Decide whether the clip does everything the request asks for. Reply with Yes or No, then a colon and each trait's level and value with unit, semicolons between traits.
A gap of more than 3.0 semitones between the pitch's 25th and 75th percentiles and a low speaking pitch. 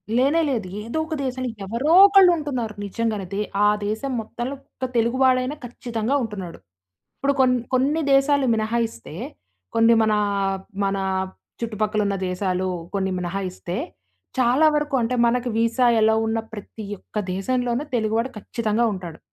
No: average, 3.5 semitones; high, 230 Hz